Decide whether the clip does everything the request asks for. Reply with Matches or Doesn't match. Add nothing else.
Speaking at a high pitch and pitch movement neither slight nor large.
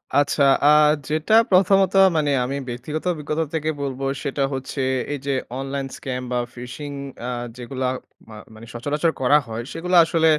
Doesn't match